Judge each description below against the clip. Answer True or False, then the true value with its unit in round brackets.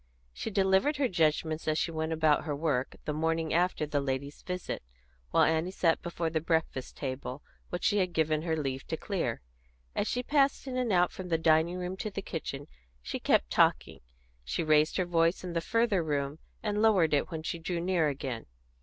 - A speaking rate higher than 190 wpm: True (200 wpm)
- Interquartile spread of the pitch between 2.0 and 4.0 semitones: True (3.2 semitones)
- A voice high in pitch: False (165 Hz)